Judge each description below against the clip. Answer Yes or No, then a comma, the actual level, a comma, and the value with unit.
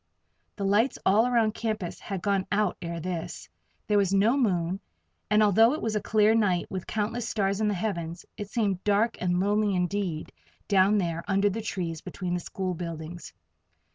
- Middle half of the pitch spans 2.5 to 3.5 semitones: Yes, average, 3.1 semitones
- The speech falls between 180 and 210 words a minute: Yes, average, 185 wpm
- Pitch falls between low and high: No, high, 200 Hz